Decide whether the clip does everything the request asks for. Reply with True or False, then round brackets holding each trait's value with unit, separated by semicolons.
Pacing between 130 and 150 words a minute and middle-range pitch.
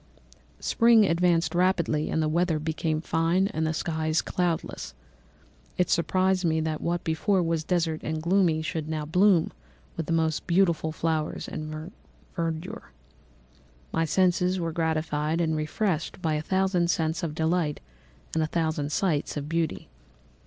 True (145 wpm; 165 Hz)